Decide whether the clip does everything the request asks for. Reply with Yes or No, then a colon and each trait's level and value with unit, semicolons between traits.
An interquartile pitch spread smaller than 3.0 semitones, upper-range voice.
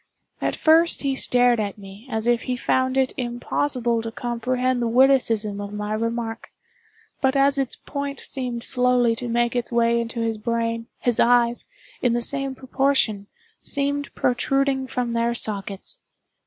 Yes: narrow, 2.4 semitones; high, 240 Hz